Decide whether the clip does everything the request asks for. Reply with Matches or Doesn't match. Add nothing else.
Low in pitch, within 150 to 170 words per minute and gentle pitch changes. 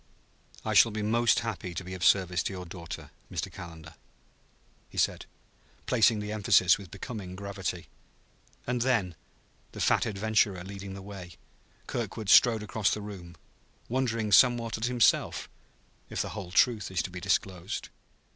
Doesn't match